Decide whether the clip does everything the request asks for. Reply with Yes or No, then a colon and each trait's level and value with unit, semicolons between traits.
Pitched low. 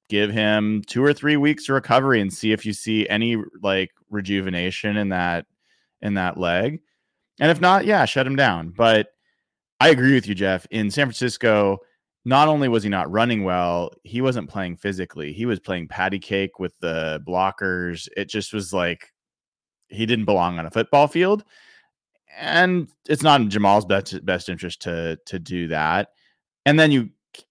Yes: low, 105 Hz